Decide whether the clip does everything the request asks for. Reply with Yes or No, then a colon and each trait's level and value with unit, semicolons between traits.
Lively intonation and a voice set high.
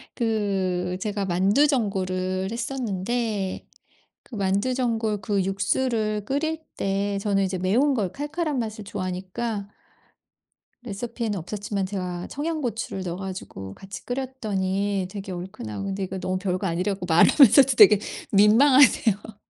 No: average, 3.7 semitones; high, 200 Hz